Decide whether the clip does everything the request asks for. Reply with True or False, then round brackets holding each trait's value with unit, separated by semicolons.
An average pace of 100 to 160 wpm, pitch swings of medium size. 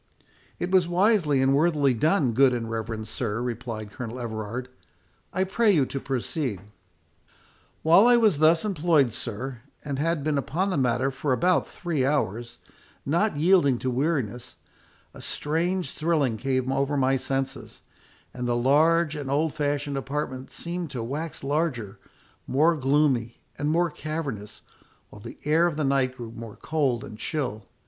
True (155 wpm; 4.6 semitones)